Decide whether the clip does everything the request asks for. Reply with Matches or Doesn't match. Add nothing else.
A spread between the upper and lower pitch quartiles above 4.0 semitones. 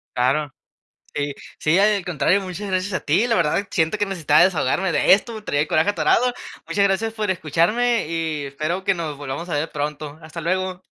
Matches